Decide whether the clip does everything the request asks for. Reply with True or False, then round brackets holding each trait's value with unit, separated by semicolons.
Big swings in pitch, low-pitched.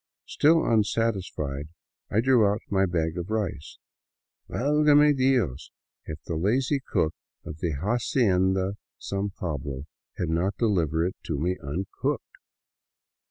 True (6.2 semitones; 95 Hz)